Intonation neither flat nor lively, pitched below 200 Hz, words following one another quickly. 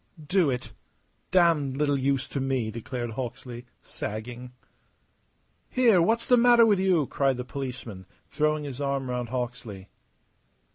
No: average, 3.9 semitones; low, 135 Hz; slow, 135 wpm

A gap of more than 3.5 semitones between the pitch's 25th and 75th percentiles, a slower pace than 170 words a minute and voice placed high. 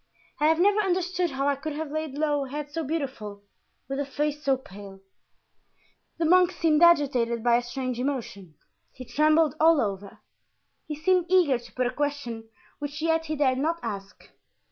No: average, 4.4 semitones; average, 180 wpm; very high, 290 Hz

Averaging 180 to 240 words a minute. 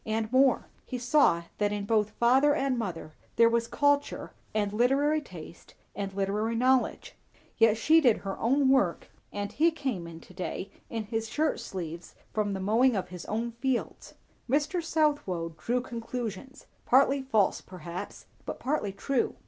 No: average, 160 wpm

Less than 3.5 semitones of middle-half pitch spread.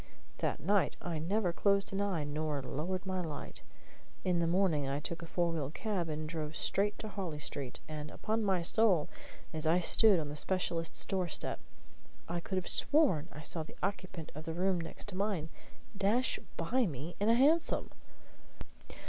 No: average, 4.2 semitones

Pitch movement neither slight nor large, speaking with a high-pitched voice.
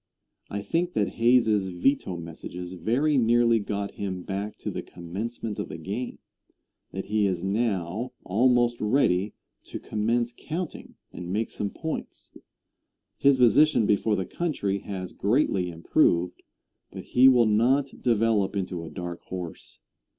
No: average, 4.6 semitones; low, 105 Hz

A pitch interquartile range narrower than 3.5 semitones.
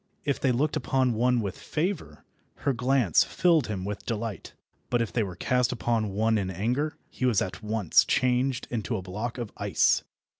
No: average, 3.8 semitones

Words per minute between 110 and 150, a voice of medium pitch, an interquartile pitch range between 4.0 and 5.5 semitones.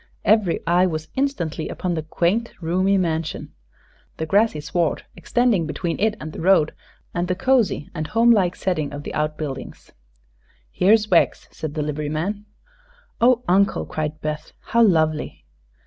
Yes: average, 145 wpm; medium, 175 Hz; average, 4.9 semitones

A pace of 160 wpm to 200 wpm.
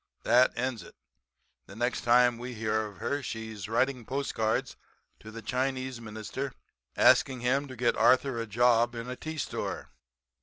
Yes: average, 165 wpm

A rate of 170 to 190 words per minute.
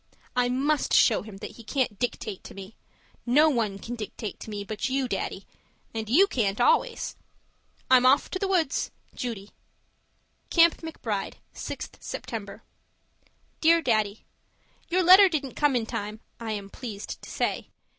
No: average, 155 wpm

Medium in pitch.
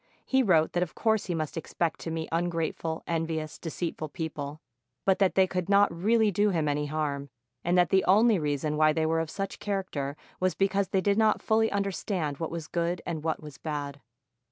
Yes: medium, 170 Hz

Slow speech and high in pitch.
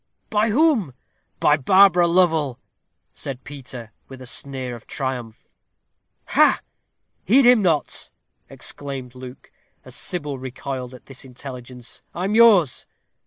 No: slow, 120 wpm; medium, 140 Hz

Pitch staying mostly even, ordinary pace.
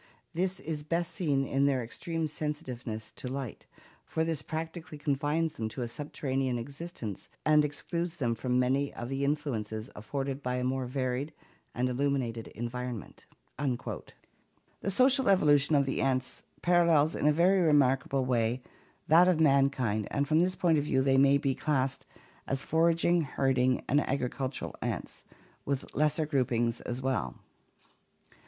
No: average, 3.5 semitones; average, 150 wpm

